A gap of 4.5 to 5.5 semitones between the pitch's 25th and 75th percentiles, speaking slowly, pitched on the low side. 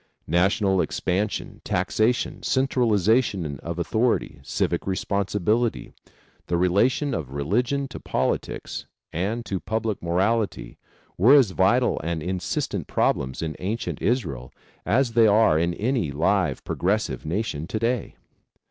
Yes: average, 5.2 semitones; slow, 120 wpm; low, 100 Hz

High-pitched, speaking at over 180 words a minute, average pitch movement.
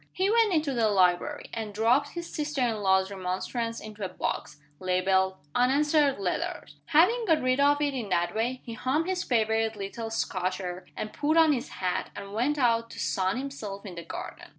No: high, 230 Hz; average, 195 wpm; wide, 6.9 semitones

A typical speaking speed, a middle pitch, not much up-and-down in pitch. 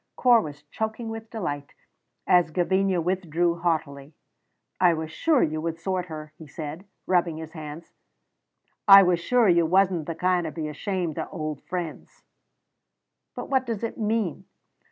No: average, 155 wpm; medium, 175 Hz; average, 3.7 semitones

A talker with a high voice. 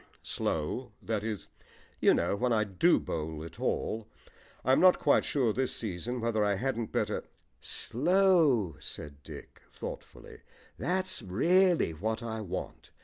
No: low, 110 Hz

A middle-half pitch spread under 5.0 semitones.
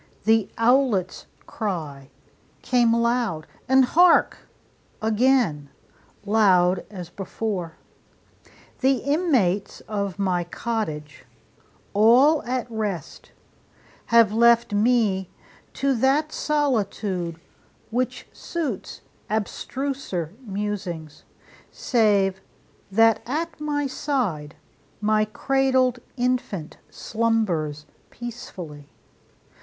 No: wide, 5.4 semitones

